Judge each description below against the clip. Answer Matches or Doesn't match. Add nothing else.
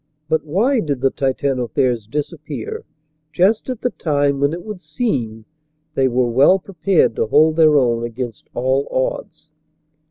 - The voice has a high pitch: Doesn't match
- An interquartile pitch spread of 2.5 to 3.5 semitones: Doesn't match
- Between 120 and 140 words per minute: Doesn't match